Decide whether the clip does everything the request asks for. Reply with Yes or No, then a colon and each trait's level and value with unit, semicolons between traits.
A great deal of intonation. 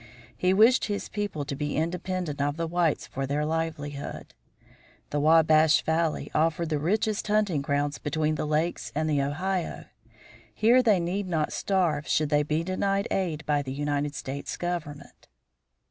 No: average, 3.7 semitones